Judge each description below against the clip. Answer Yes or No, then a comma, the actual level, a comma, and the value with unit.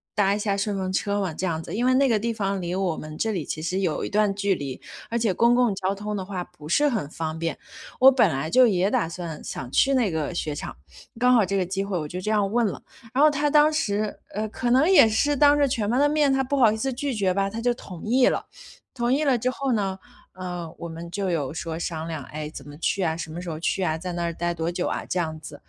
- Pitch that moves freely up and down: Yes, wide, 5.9 semitones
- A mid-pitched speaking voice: No, high, 195 Hz